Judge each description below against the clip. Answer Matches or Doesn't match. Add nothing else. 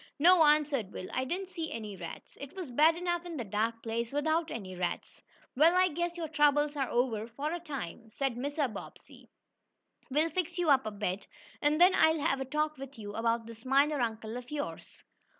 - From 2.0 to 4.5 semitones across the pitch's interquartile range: Doesn't match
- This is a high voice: Matches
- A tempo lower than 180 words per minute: Doesn't match